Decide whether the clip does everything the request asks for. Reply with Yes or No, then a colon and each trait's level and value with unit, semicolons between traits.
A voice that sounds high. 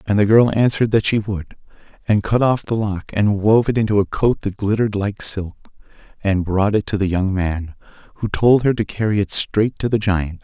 No: low, 105 Hz